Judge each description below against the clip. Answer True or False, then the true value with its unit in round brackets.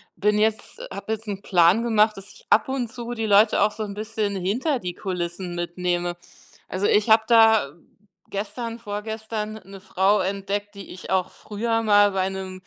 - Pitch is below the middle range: False (205 Hz)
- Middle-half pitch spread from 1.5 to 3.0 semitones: True (2.6 semitones)